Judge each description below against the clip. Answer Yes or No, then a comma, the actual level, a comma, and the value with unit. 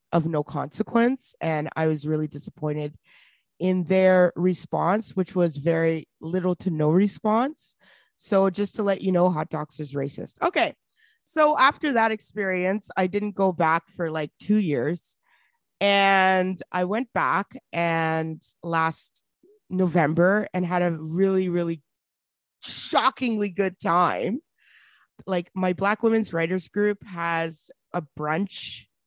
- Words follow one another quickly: No, slow, 135 wpm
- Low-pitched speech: No, medium, 185 Hz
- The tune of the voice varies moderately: Yes, average, 4.1 semitones